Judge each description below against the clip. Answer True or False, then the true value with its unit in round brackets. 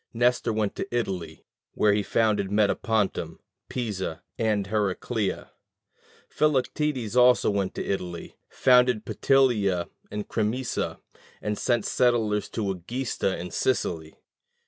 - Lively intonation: False (4.0 semitones)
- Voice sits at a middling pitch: False (105 Hz)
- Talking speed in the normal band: False (110 wpm)